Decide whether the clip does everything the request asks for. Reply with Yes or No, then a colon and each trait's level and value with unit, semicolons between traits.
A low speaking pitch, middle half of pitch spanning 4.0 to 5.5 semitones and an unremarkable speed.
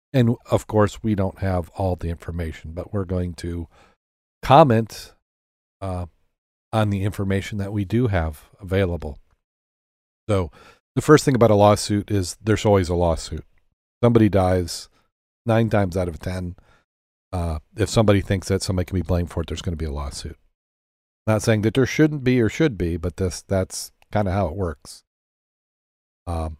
Yes: very low, 90 Hz; average, 4.5 semitones; average, 175 wpm